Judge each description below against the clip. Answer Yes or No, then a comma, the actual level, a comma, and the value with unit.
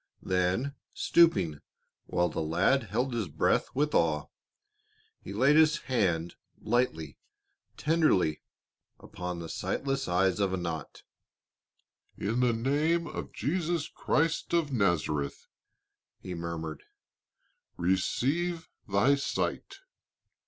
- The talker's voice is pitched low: Yes, low, 105 Hz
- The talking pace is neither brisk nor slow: No, slow, 105 wpm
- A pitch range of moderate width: No, wide, 8.5 semitones